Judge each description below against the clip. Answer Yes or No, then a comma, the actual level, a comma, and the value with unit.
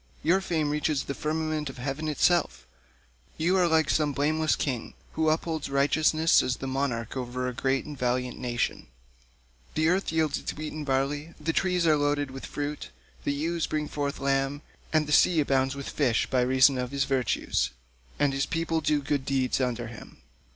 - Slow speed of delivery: No, average, 185 wpm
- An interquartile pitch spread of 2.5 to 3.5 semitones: Yes, average, 2.8 semitones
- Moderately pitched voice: Yes, medium, 145 Hz